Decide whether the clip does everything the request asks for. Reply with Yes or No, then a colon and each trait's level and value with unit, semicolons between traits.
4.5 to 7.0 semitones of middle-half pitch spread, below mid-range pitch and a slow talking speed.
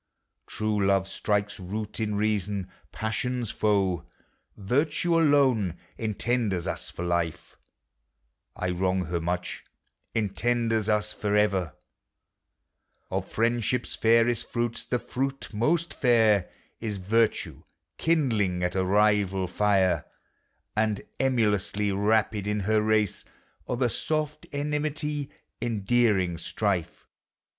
No: average, 3.7 semitones; low, 105 Hz; slow, 105 wpm